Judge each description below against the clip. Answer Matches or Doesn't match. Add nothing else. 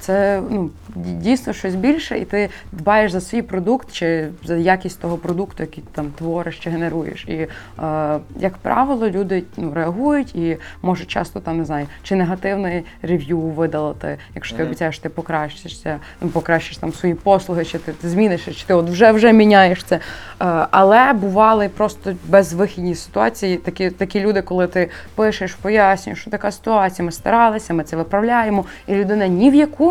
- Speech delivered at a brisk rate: Matches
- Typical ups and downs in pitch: Matches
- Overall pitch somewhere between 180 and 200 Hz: Matches